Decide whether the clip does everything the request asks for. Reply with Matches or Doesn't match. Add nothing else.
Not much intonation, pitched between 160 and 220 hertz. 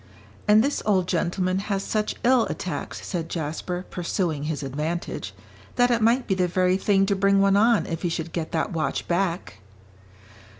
Doesn't match